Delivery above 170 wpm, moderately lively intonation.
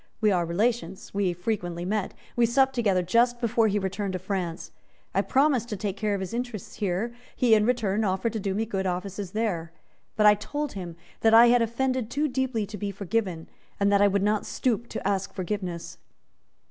Yes: average, 200 wpm; average, 3.6 semitones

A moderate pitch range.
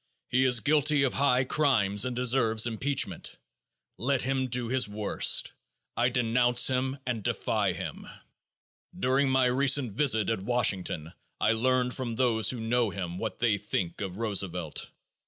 Yes: average, 3.2 semitones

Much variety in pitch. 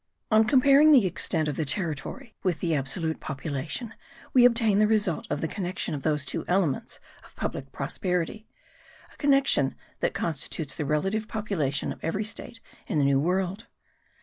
Yes: wide, 6.4 semitones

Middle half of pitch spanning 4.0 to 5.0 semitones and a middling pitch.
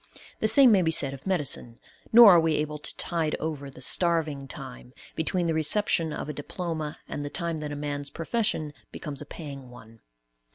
No: average, 3.0 semitones; medium, 155 Hz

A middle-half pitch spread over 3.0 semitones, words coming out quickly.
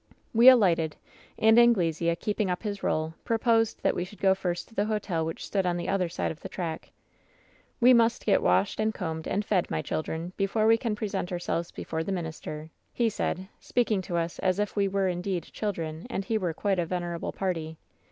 Yes: average, 4.0 semitones; fast, 220 wpm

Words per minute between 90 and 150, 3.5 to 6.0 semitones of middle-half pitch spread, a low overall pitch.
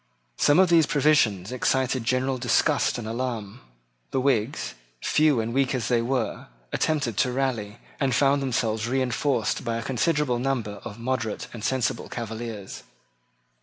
No: average, 145 wpm; average, 3.0 semitones; low, 125 Hz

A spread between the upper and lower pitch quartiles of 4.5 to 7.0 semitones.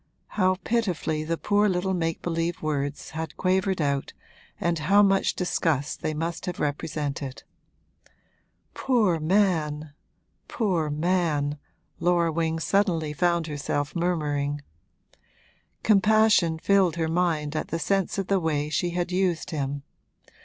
No: average, 3.5 semitones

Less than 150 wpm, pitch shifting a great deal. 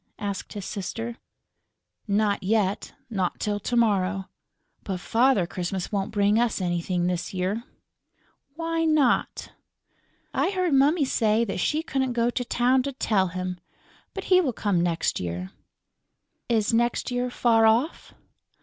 No: average, 140 wpm; average, 4.8 semitones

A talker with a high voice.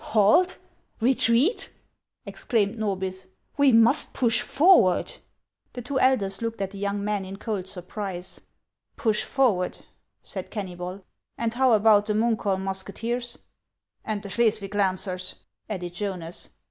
Yes: high, 210 Hz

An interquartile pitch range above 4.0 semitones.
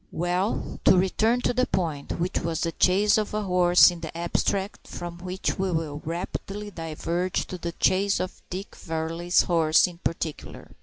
No: narrow, 2.4 semitones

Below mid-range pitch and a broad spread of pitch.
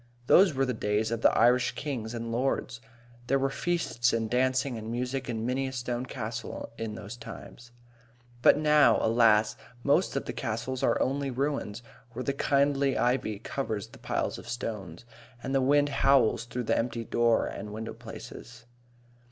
No: low, 120 Hz; average, 3.1 semitones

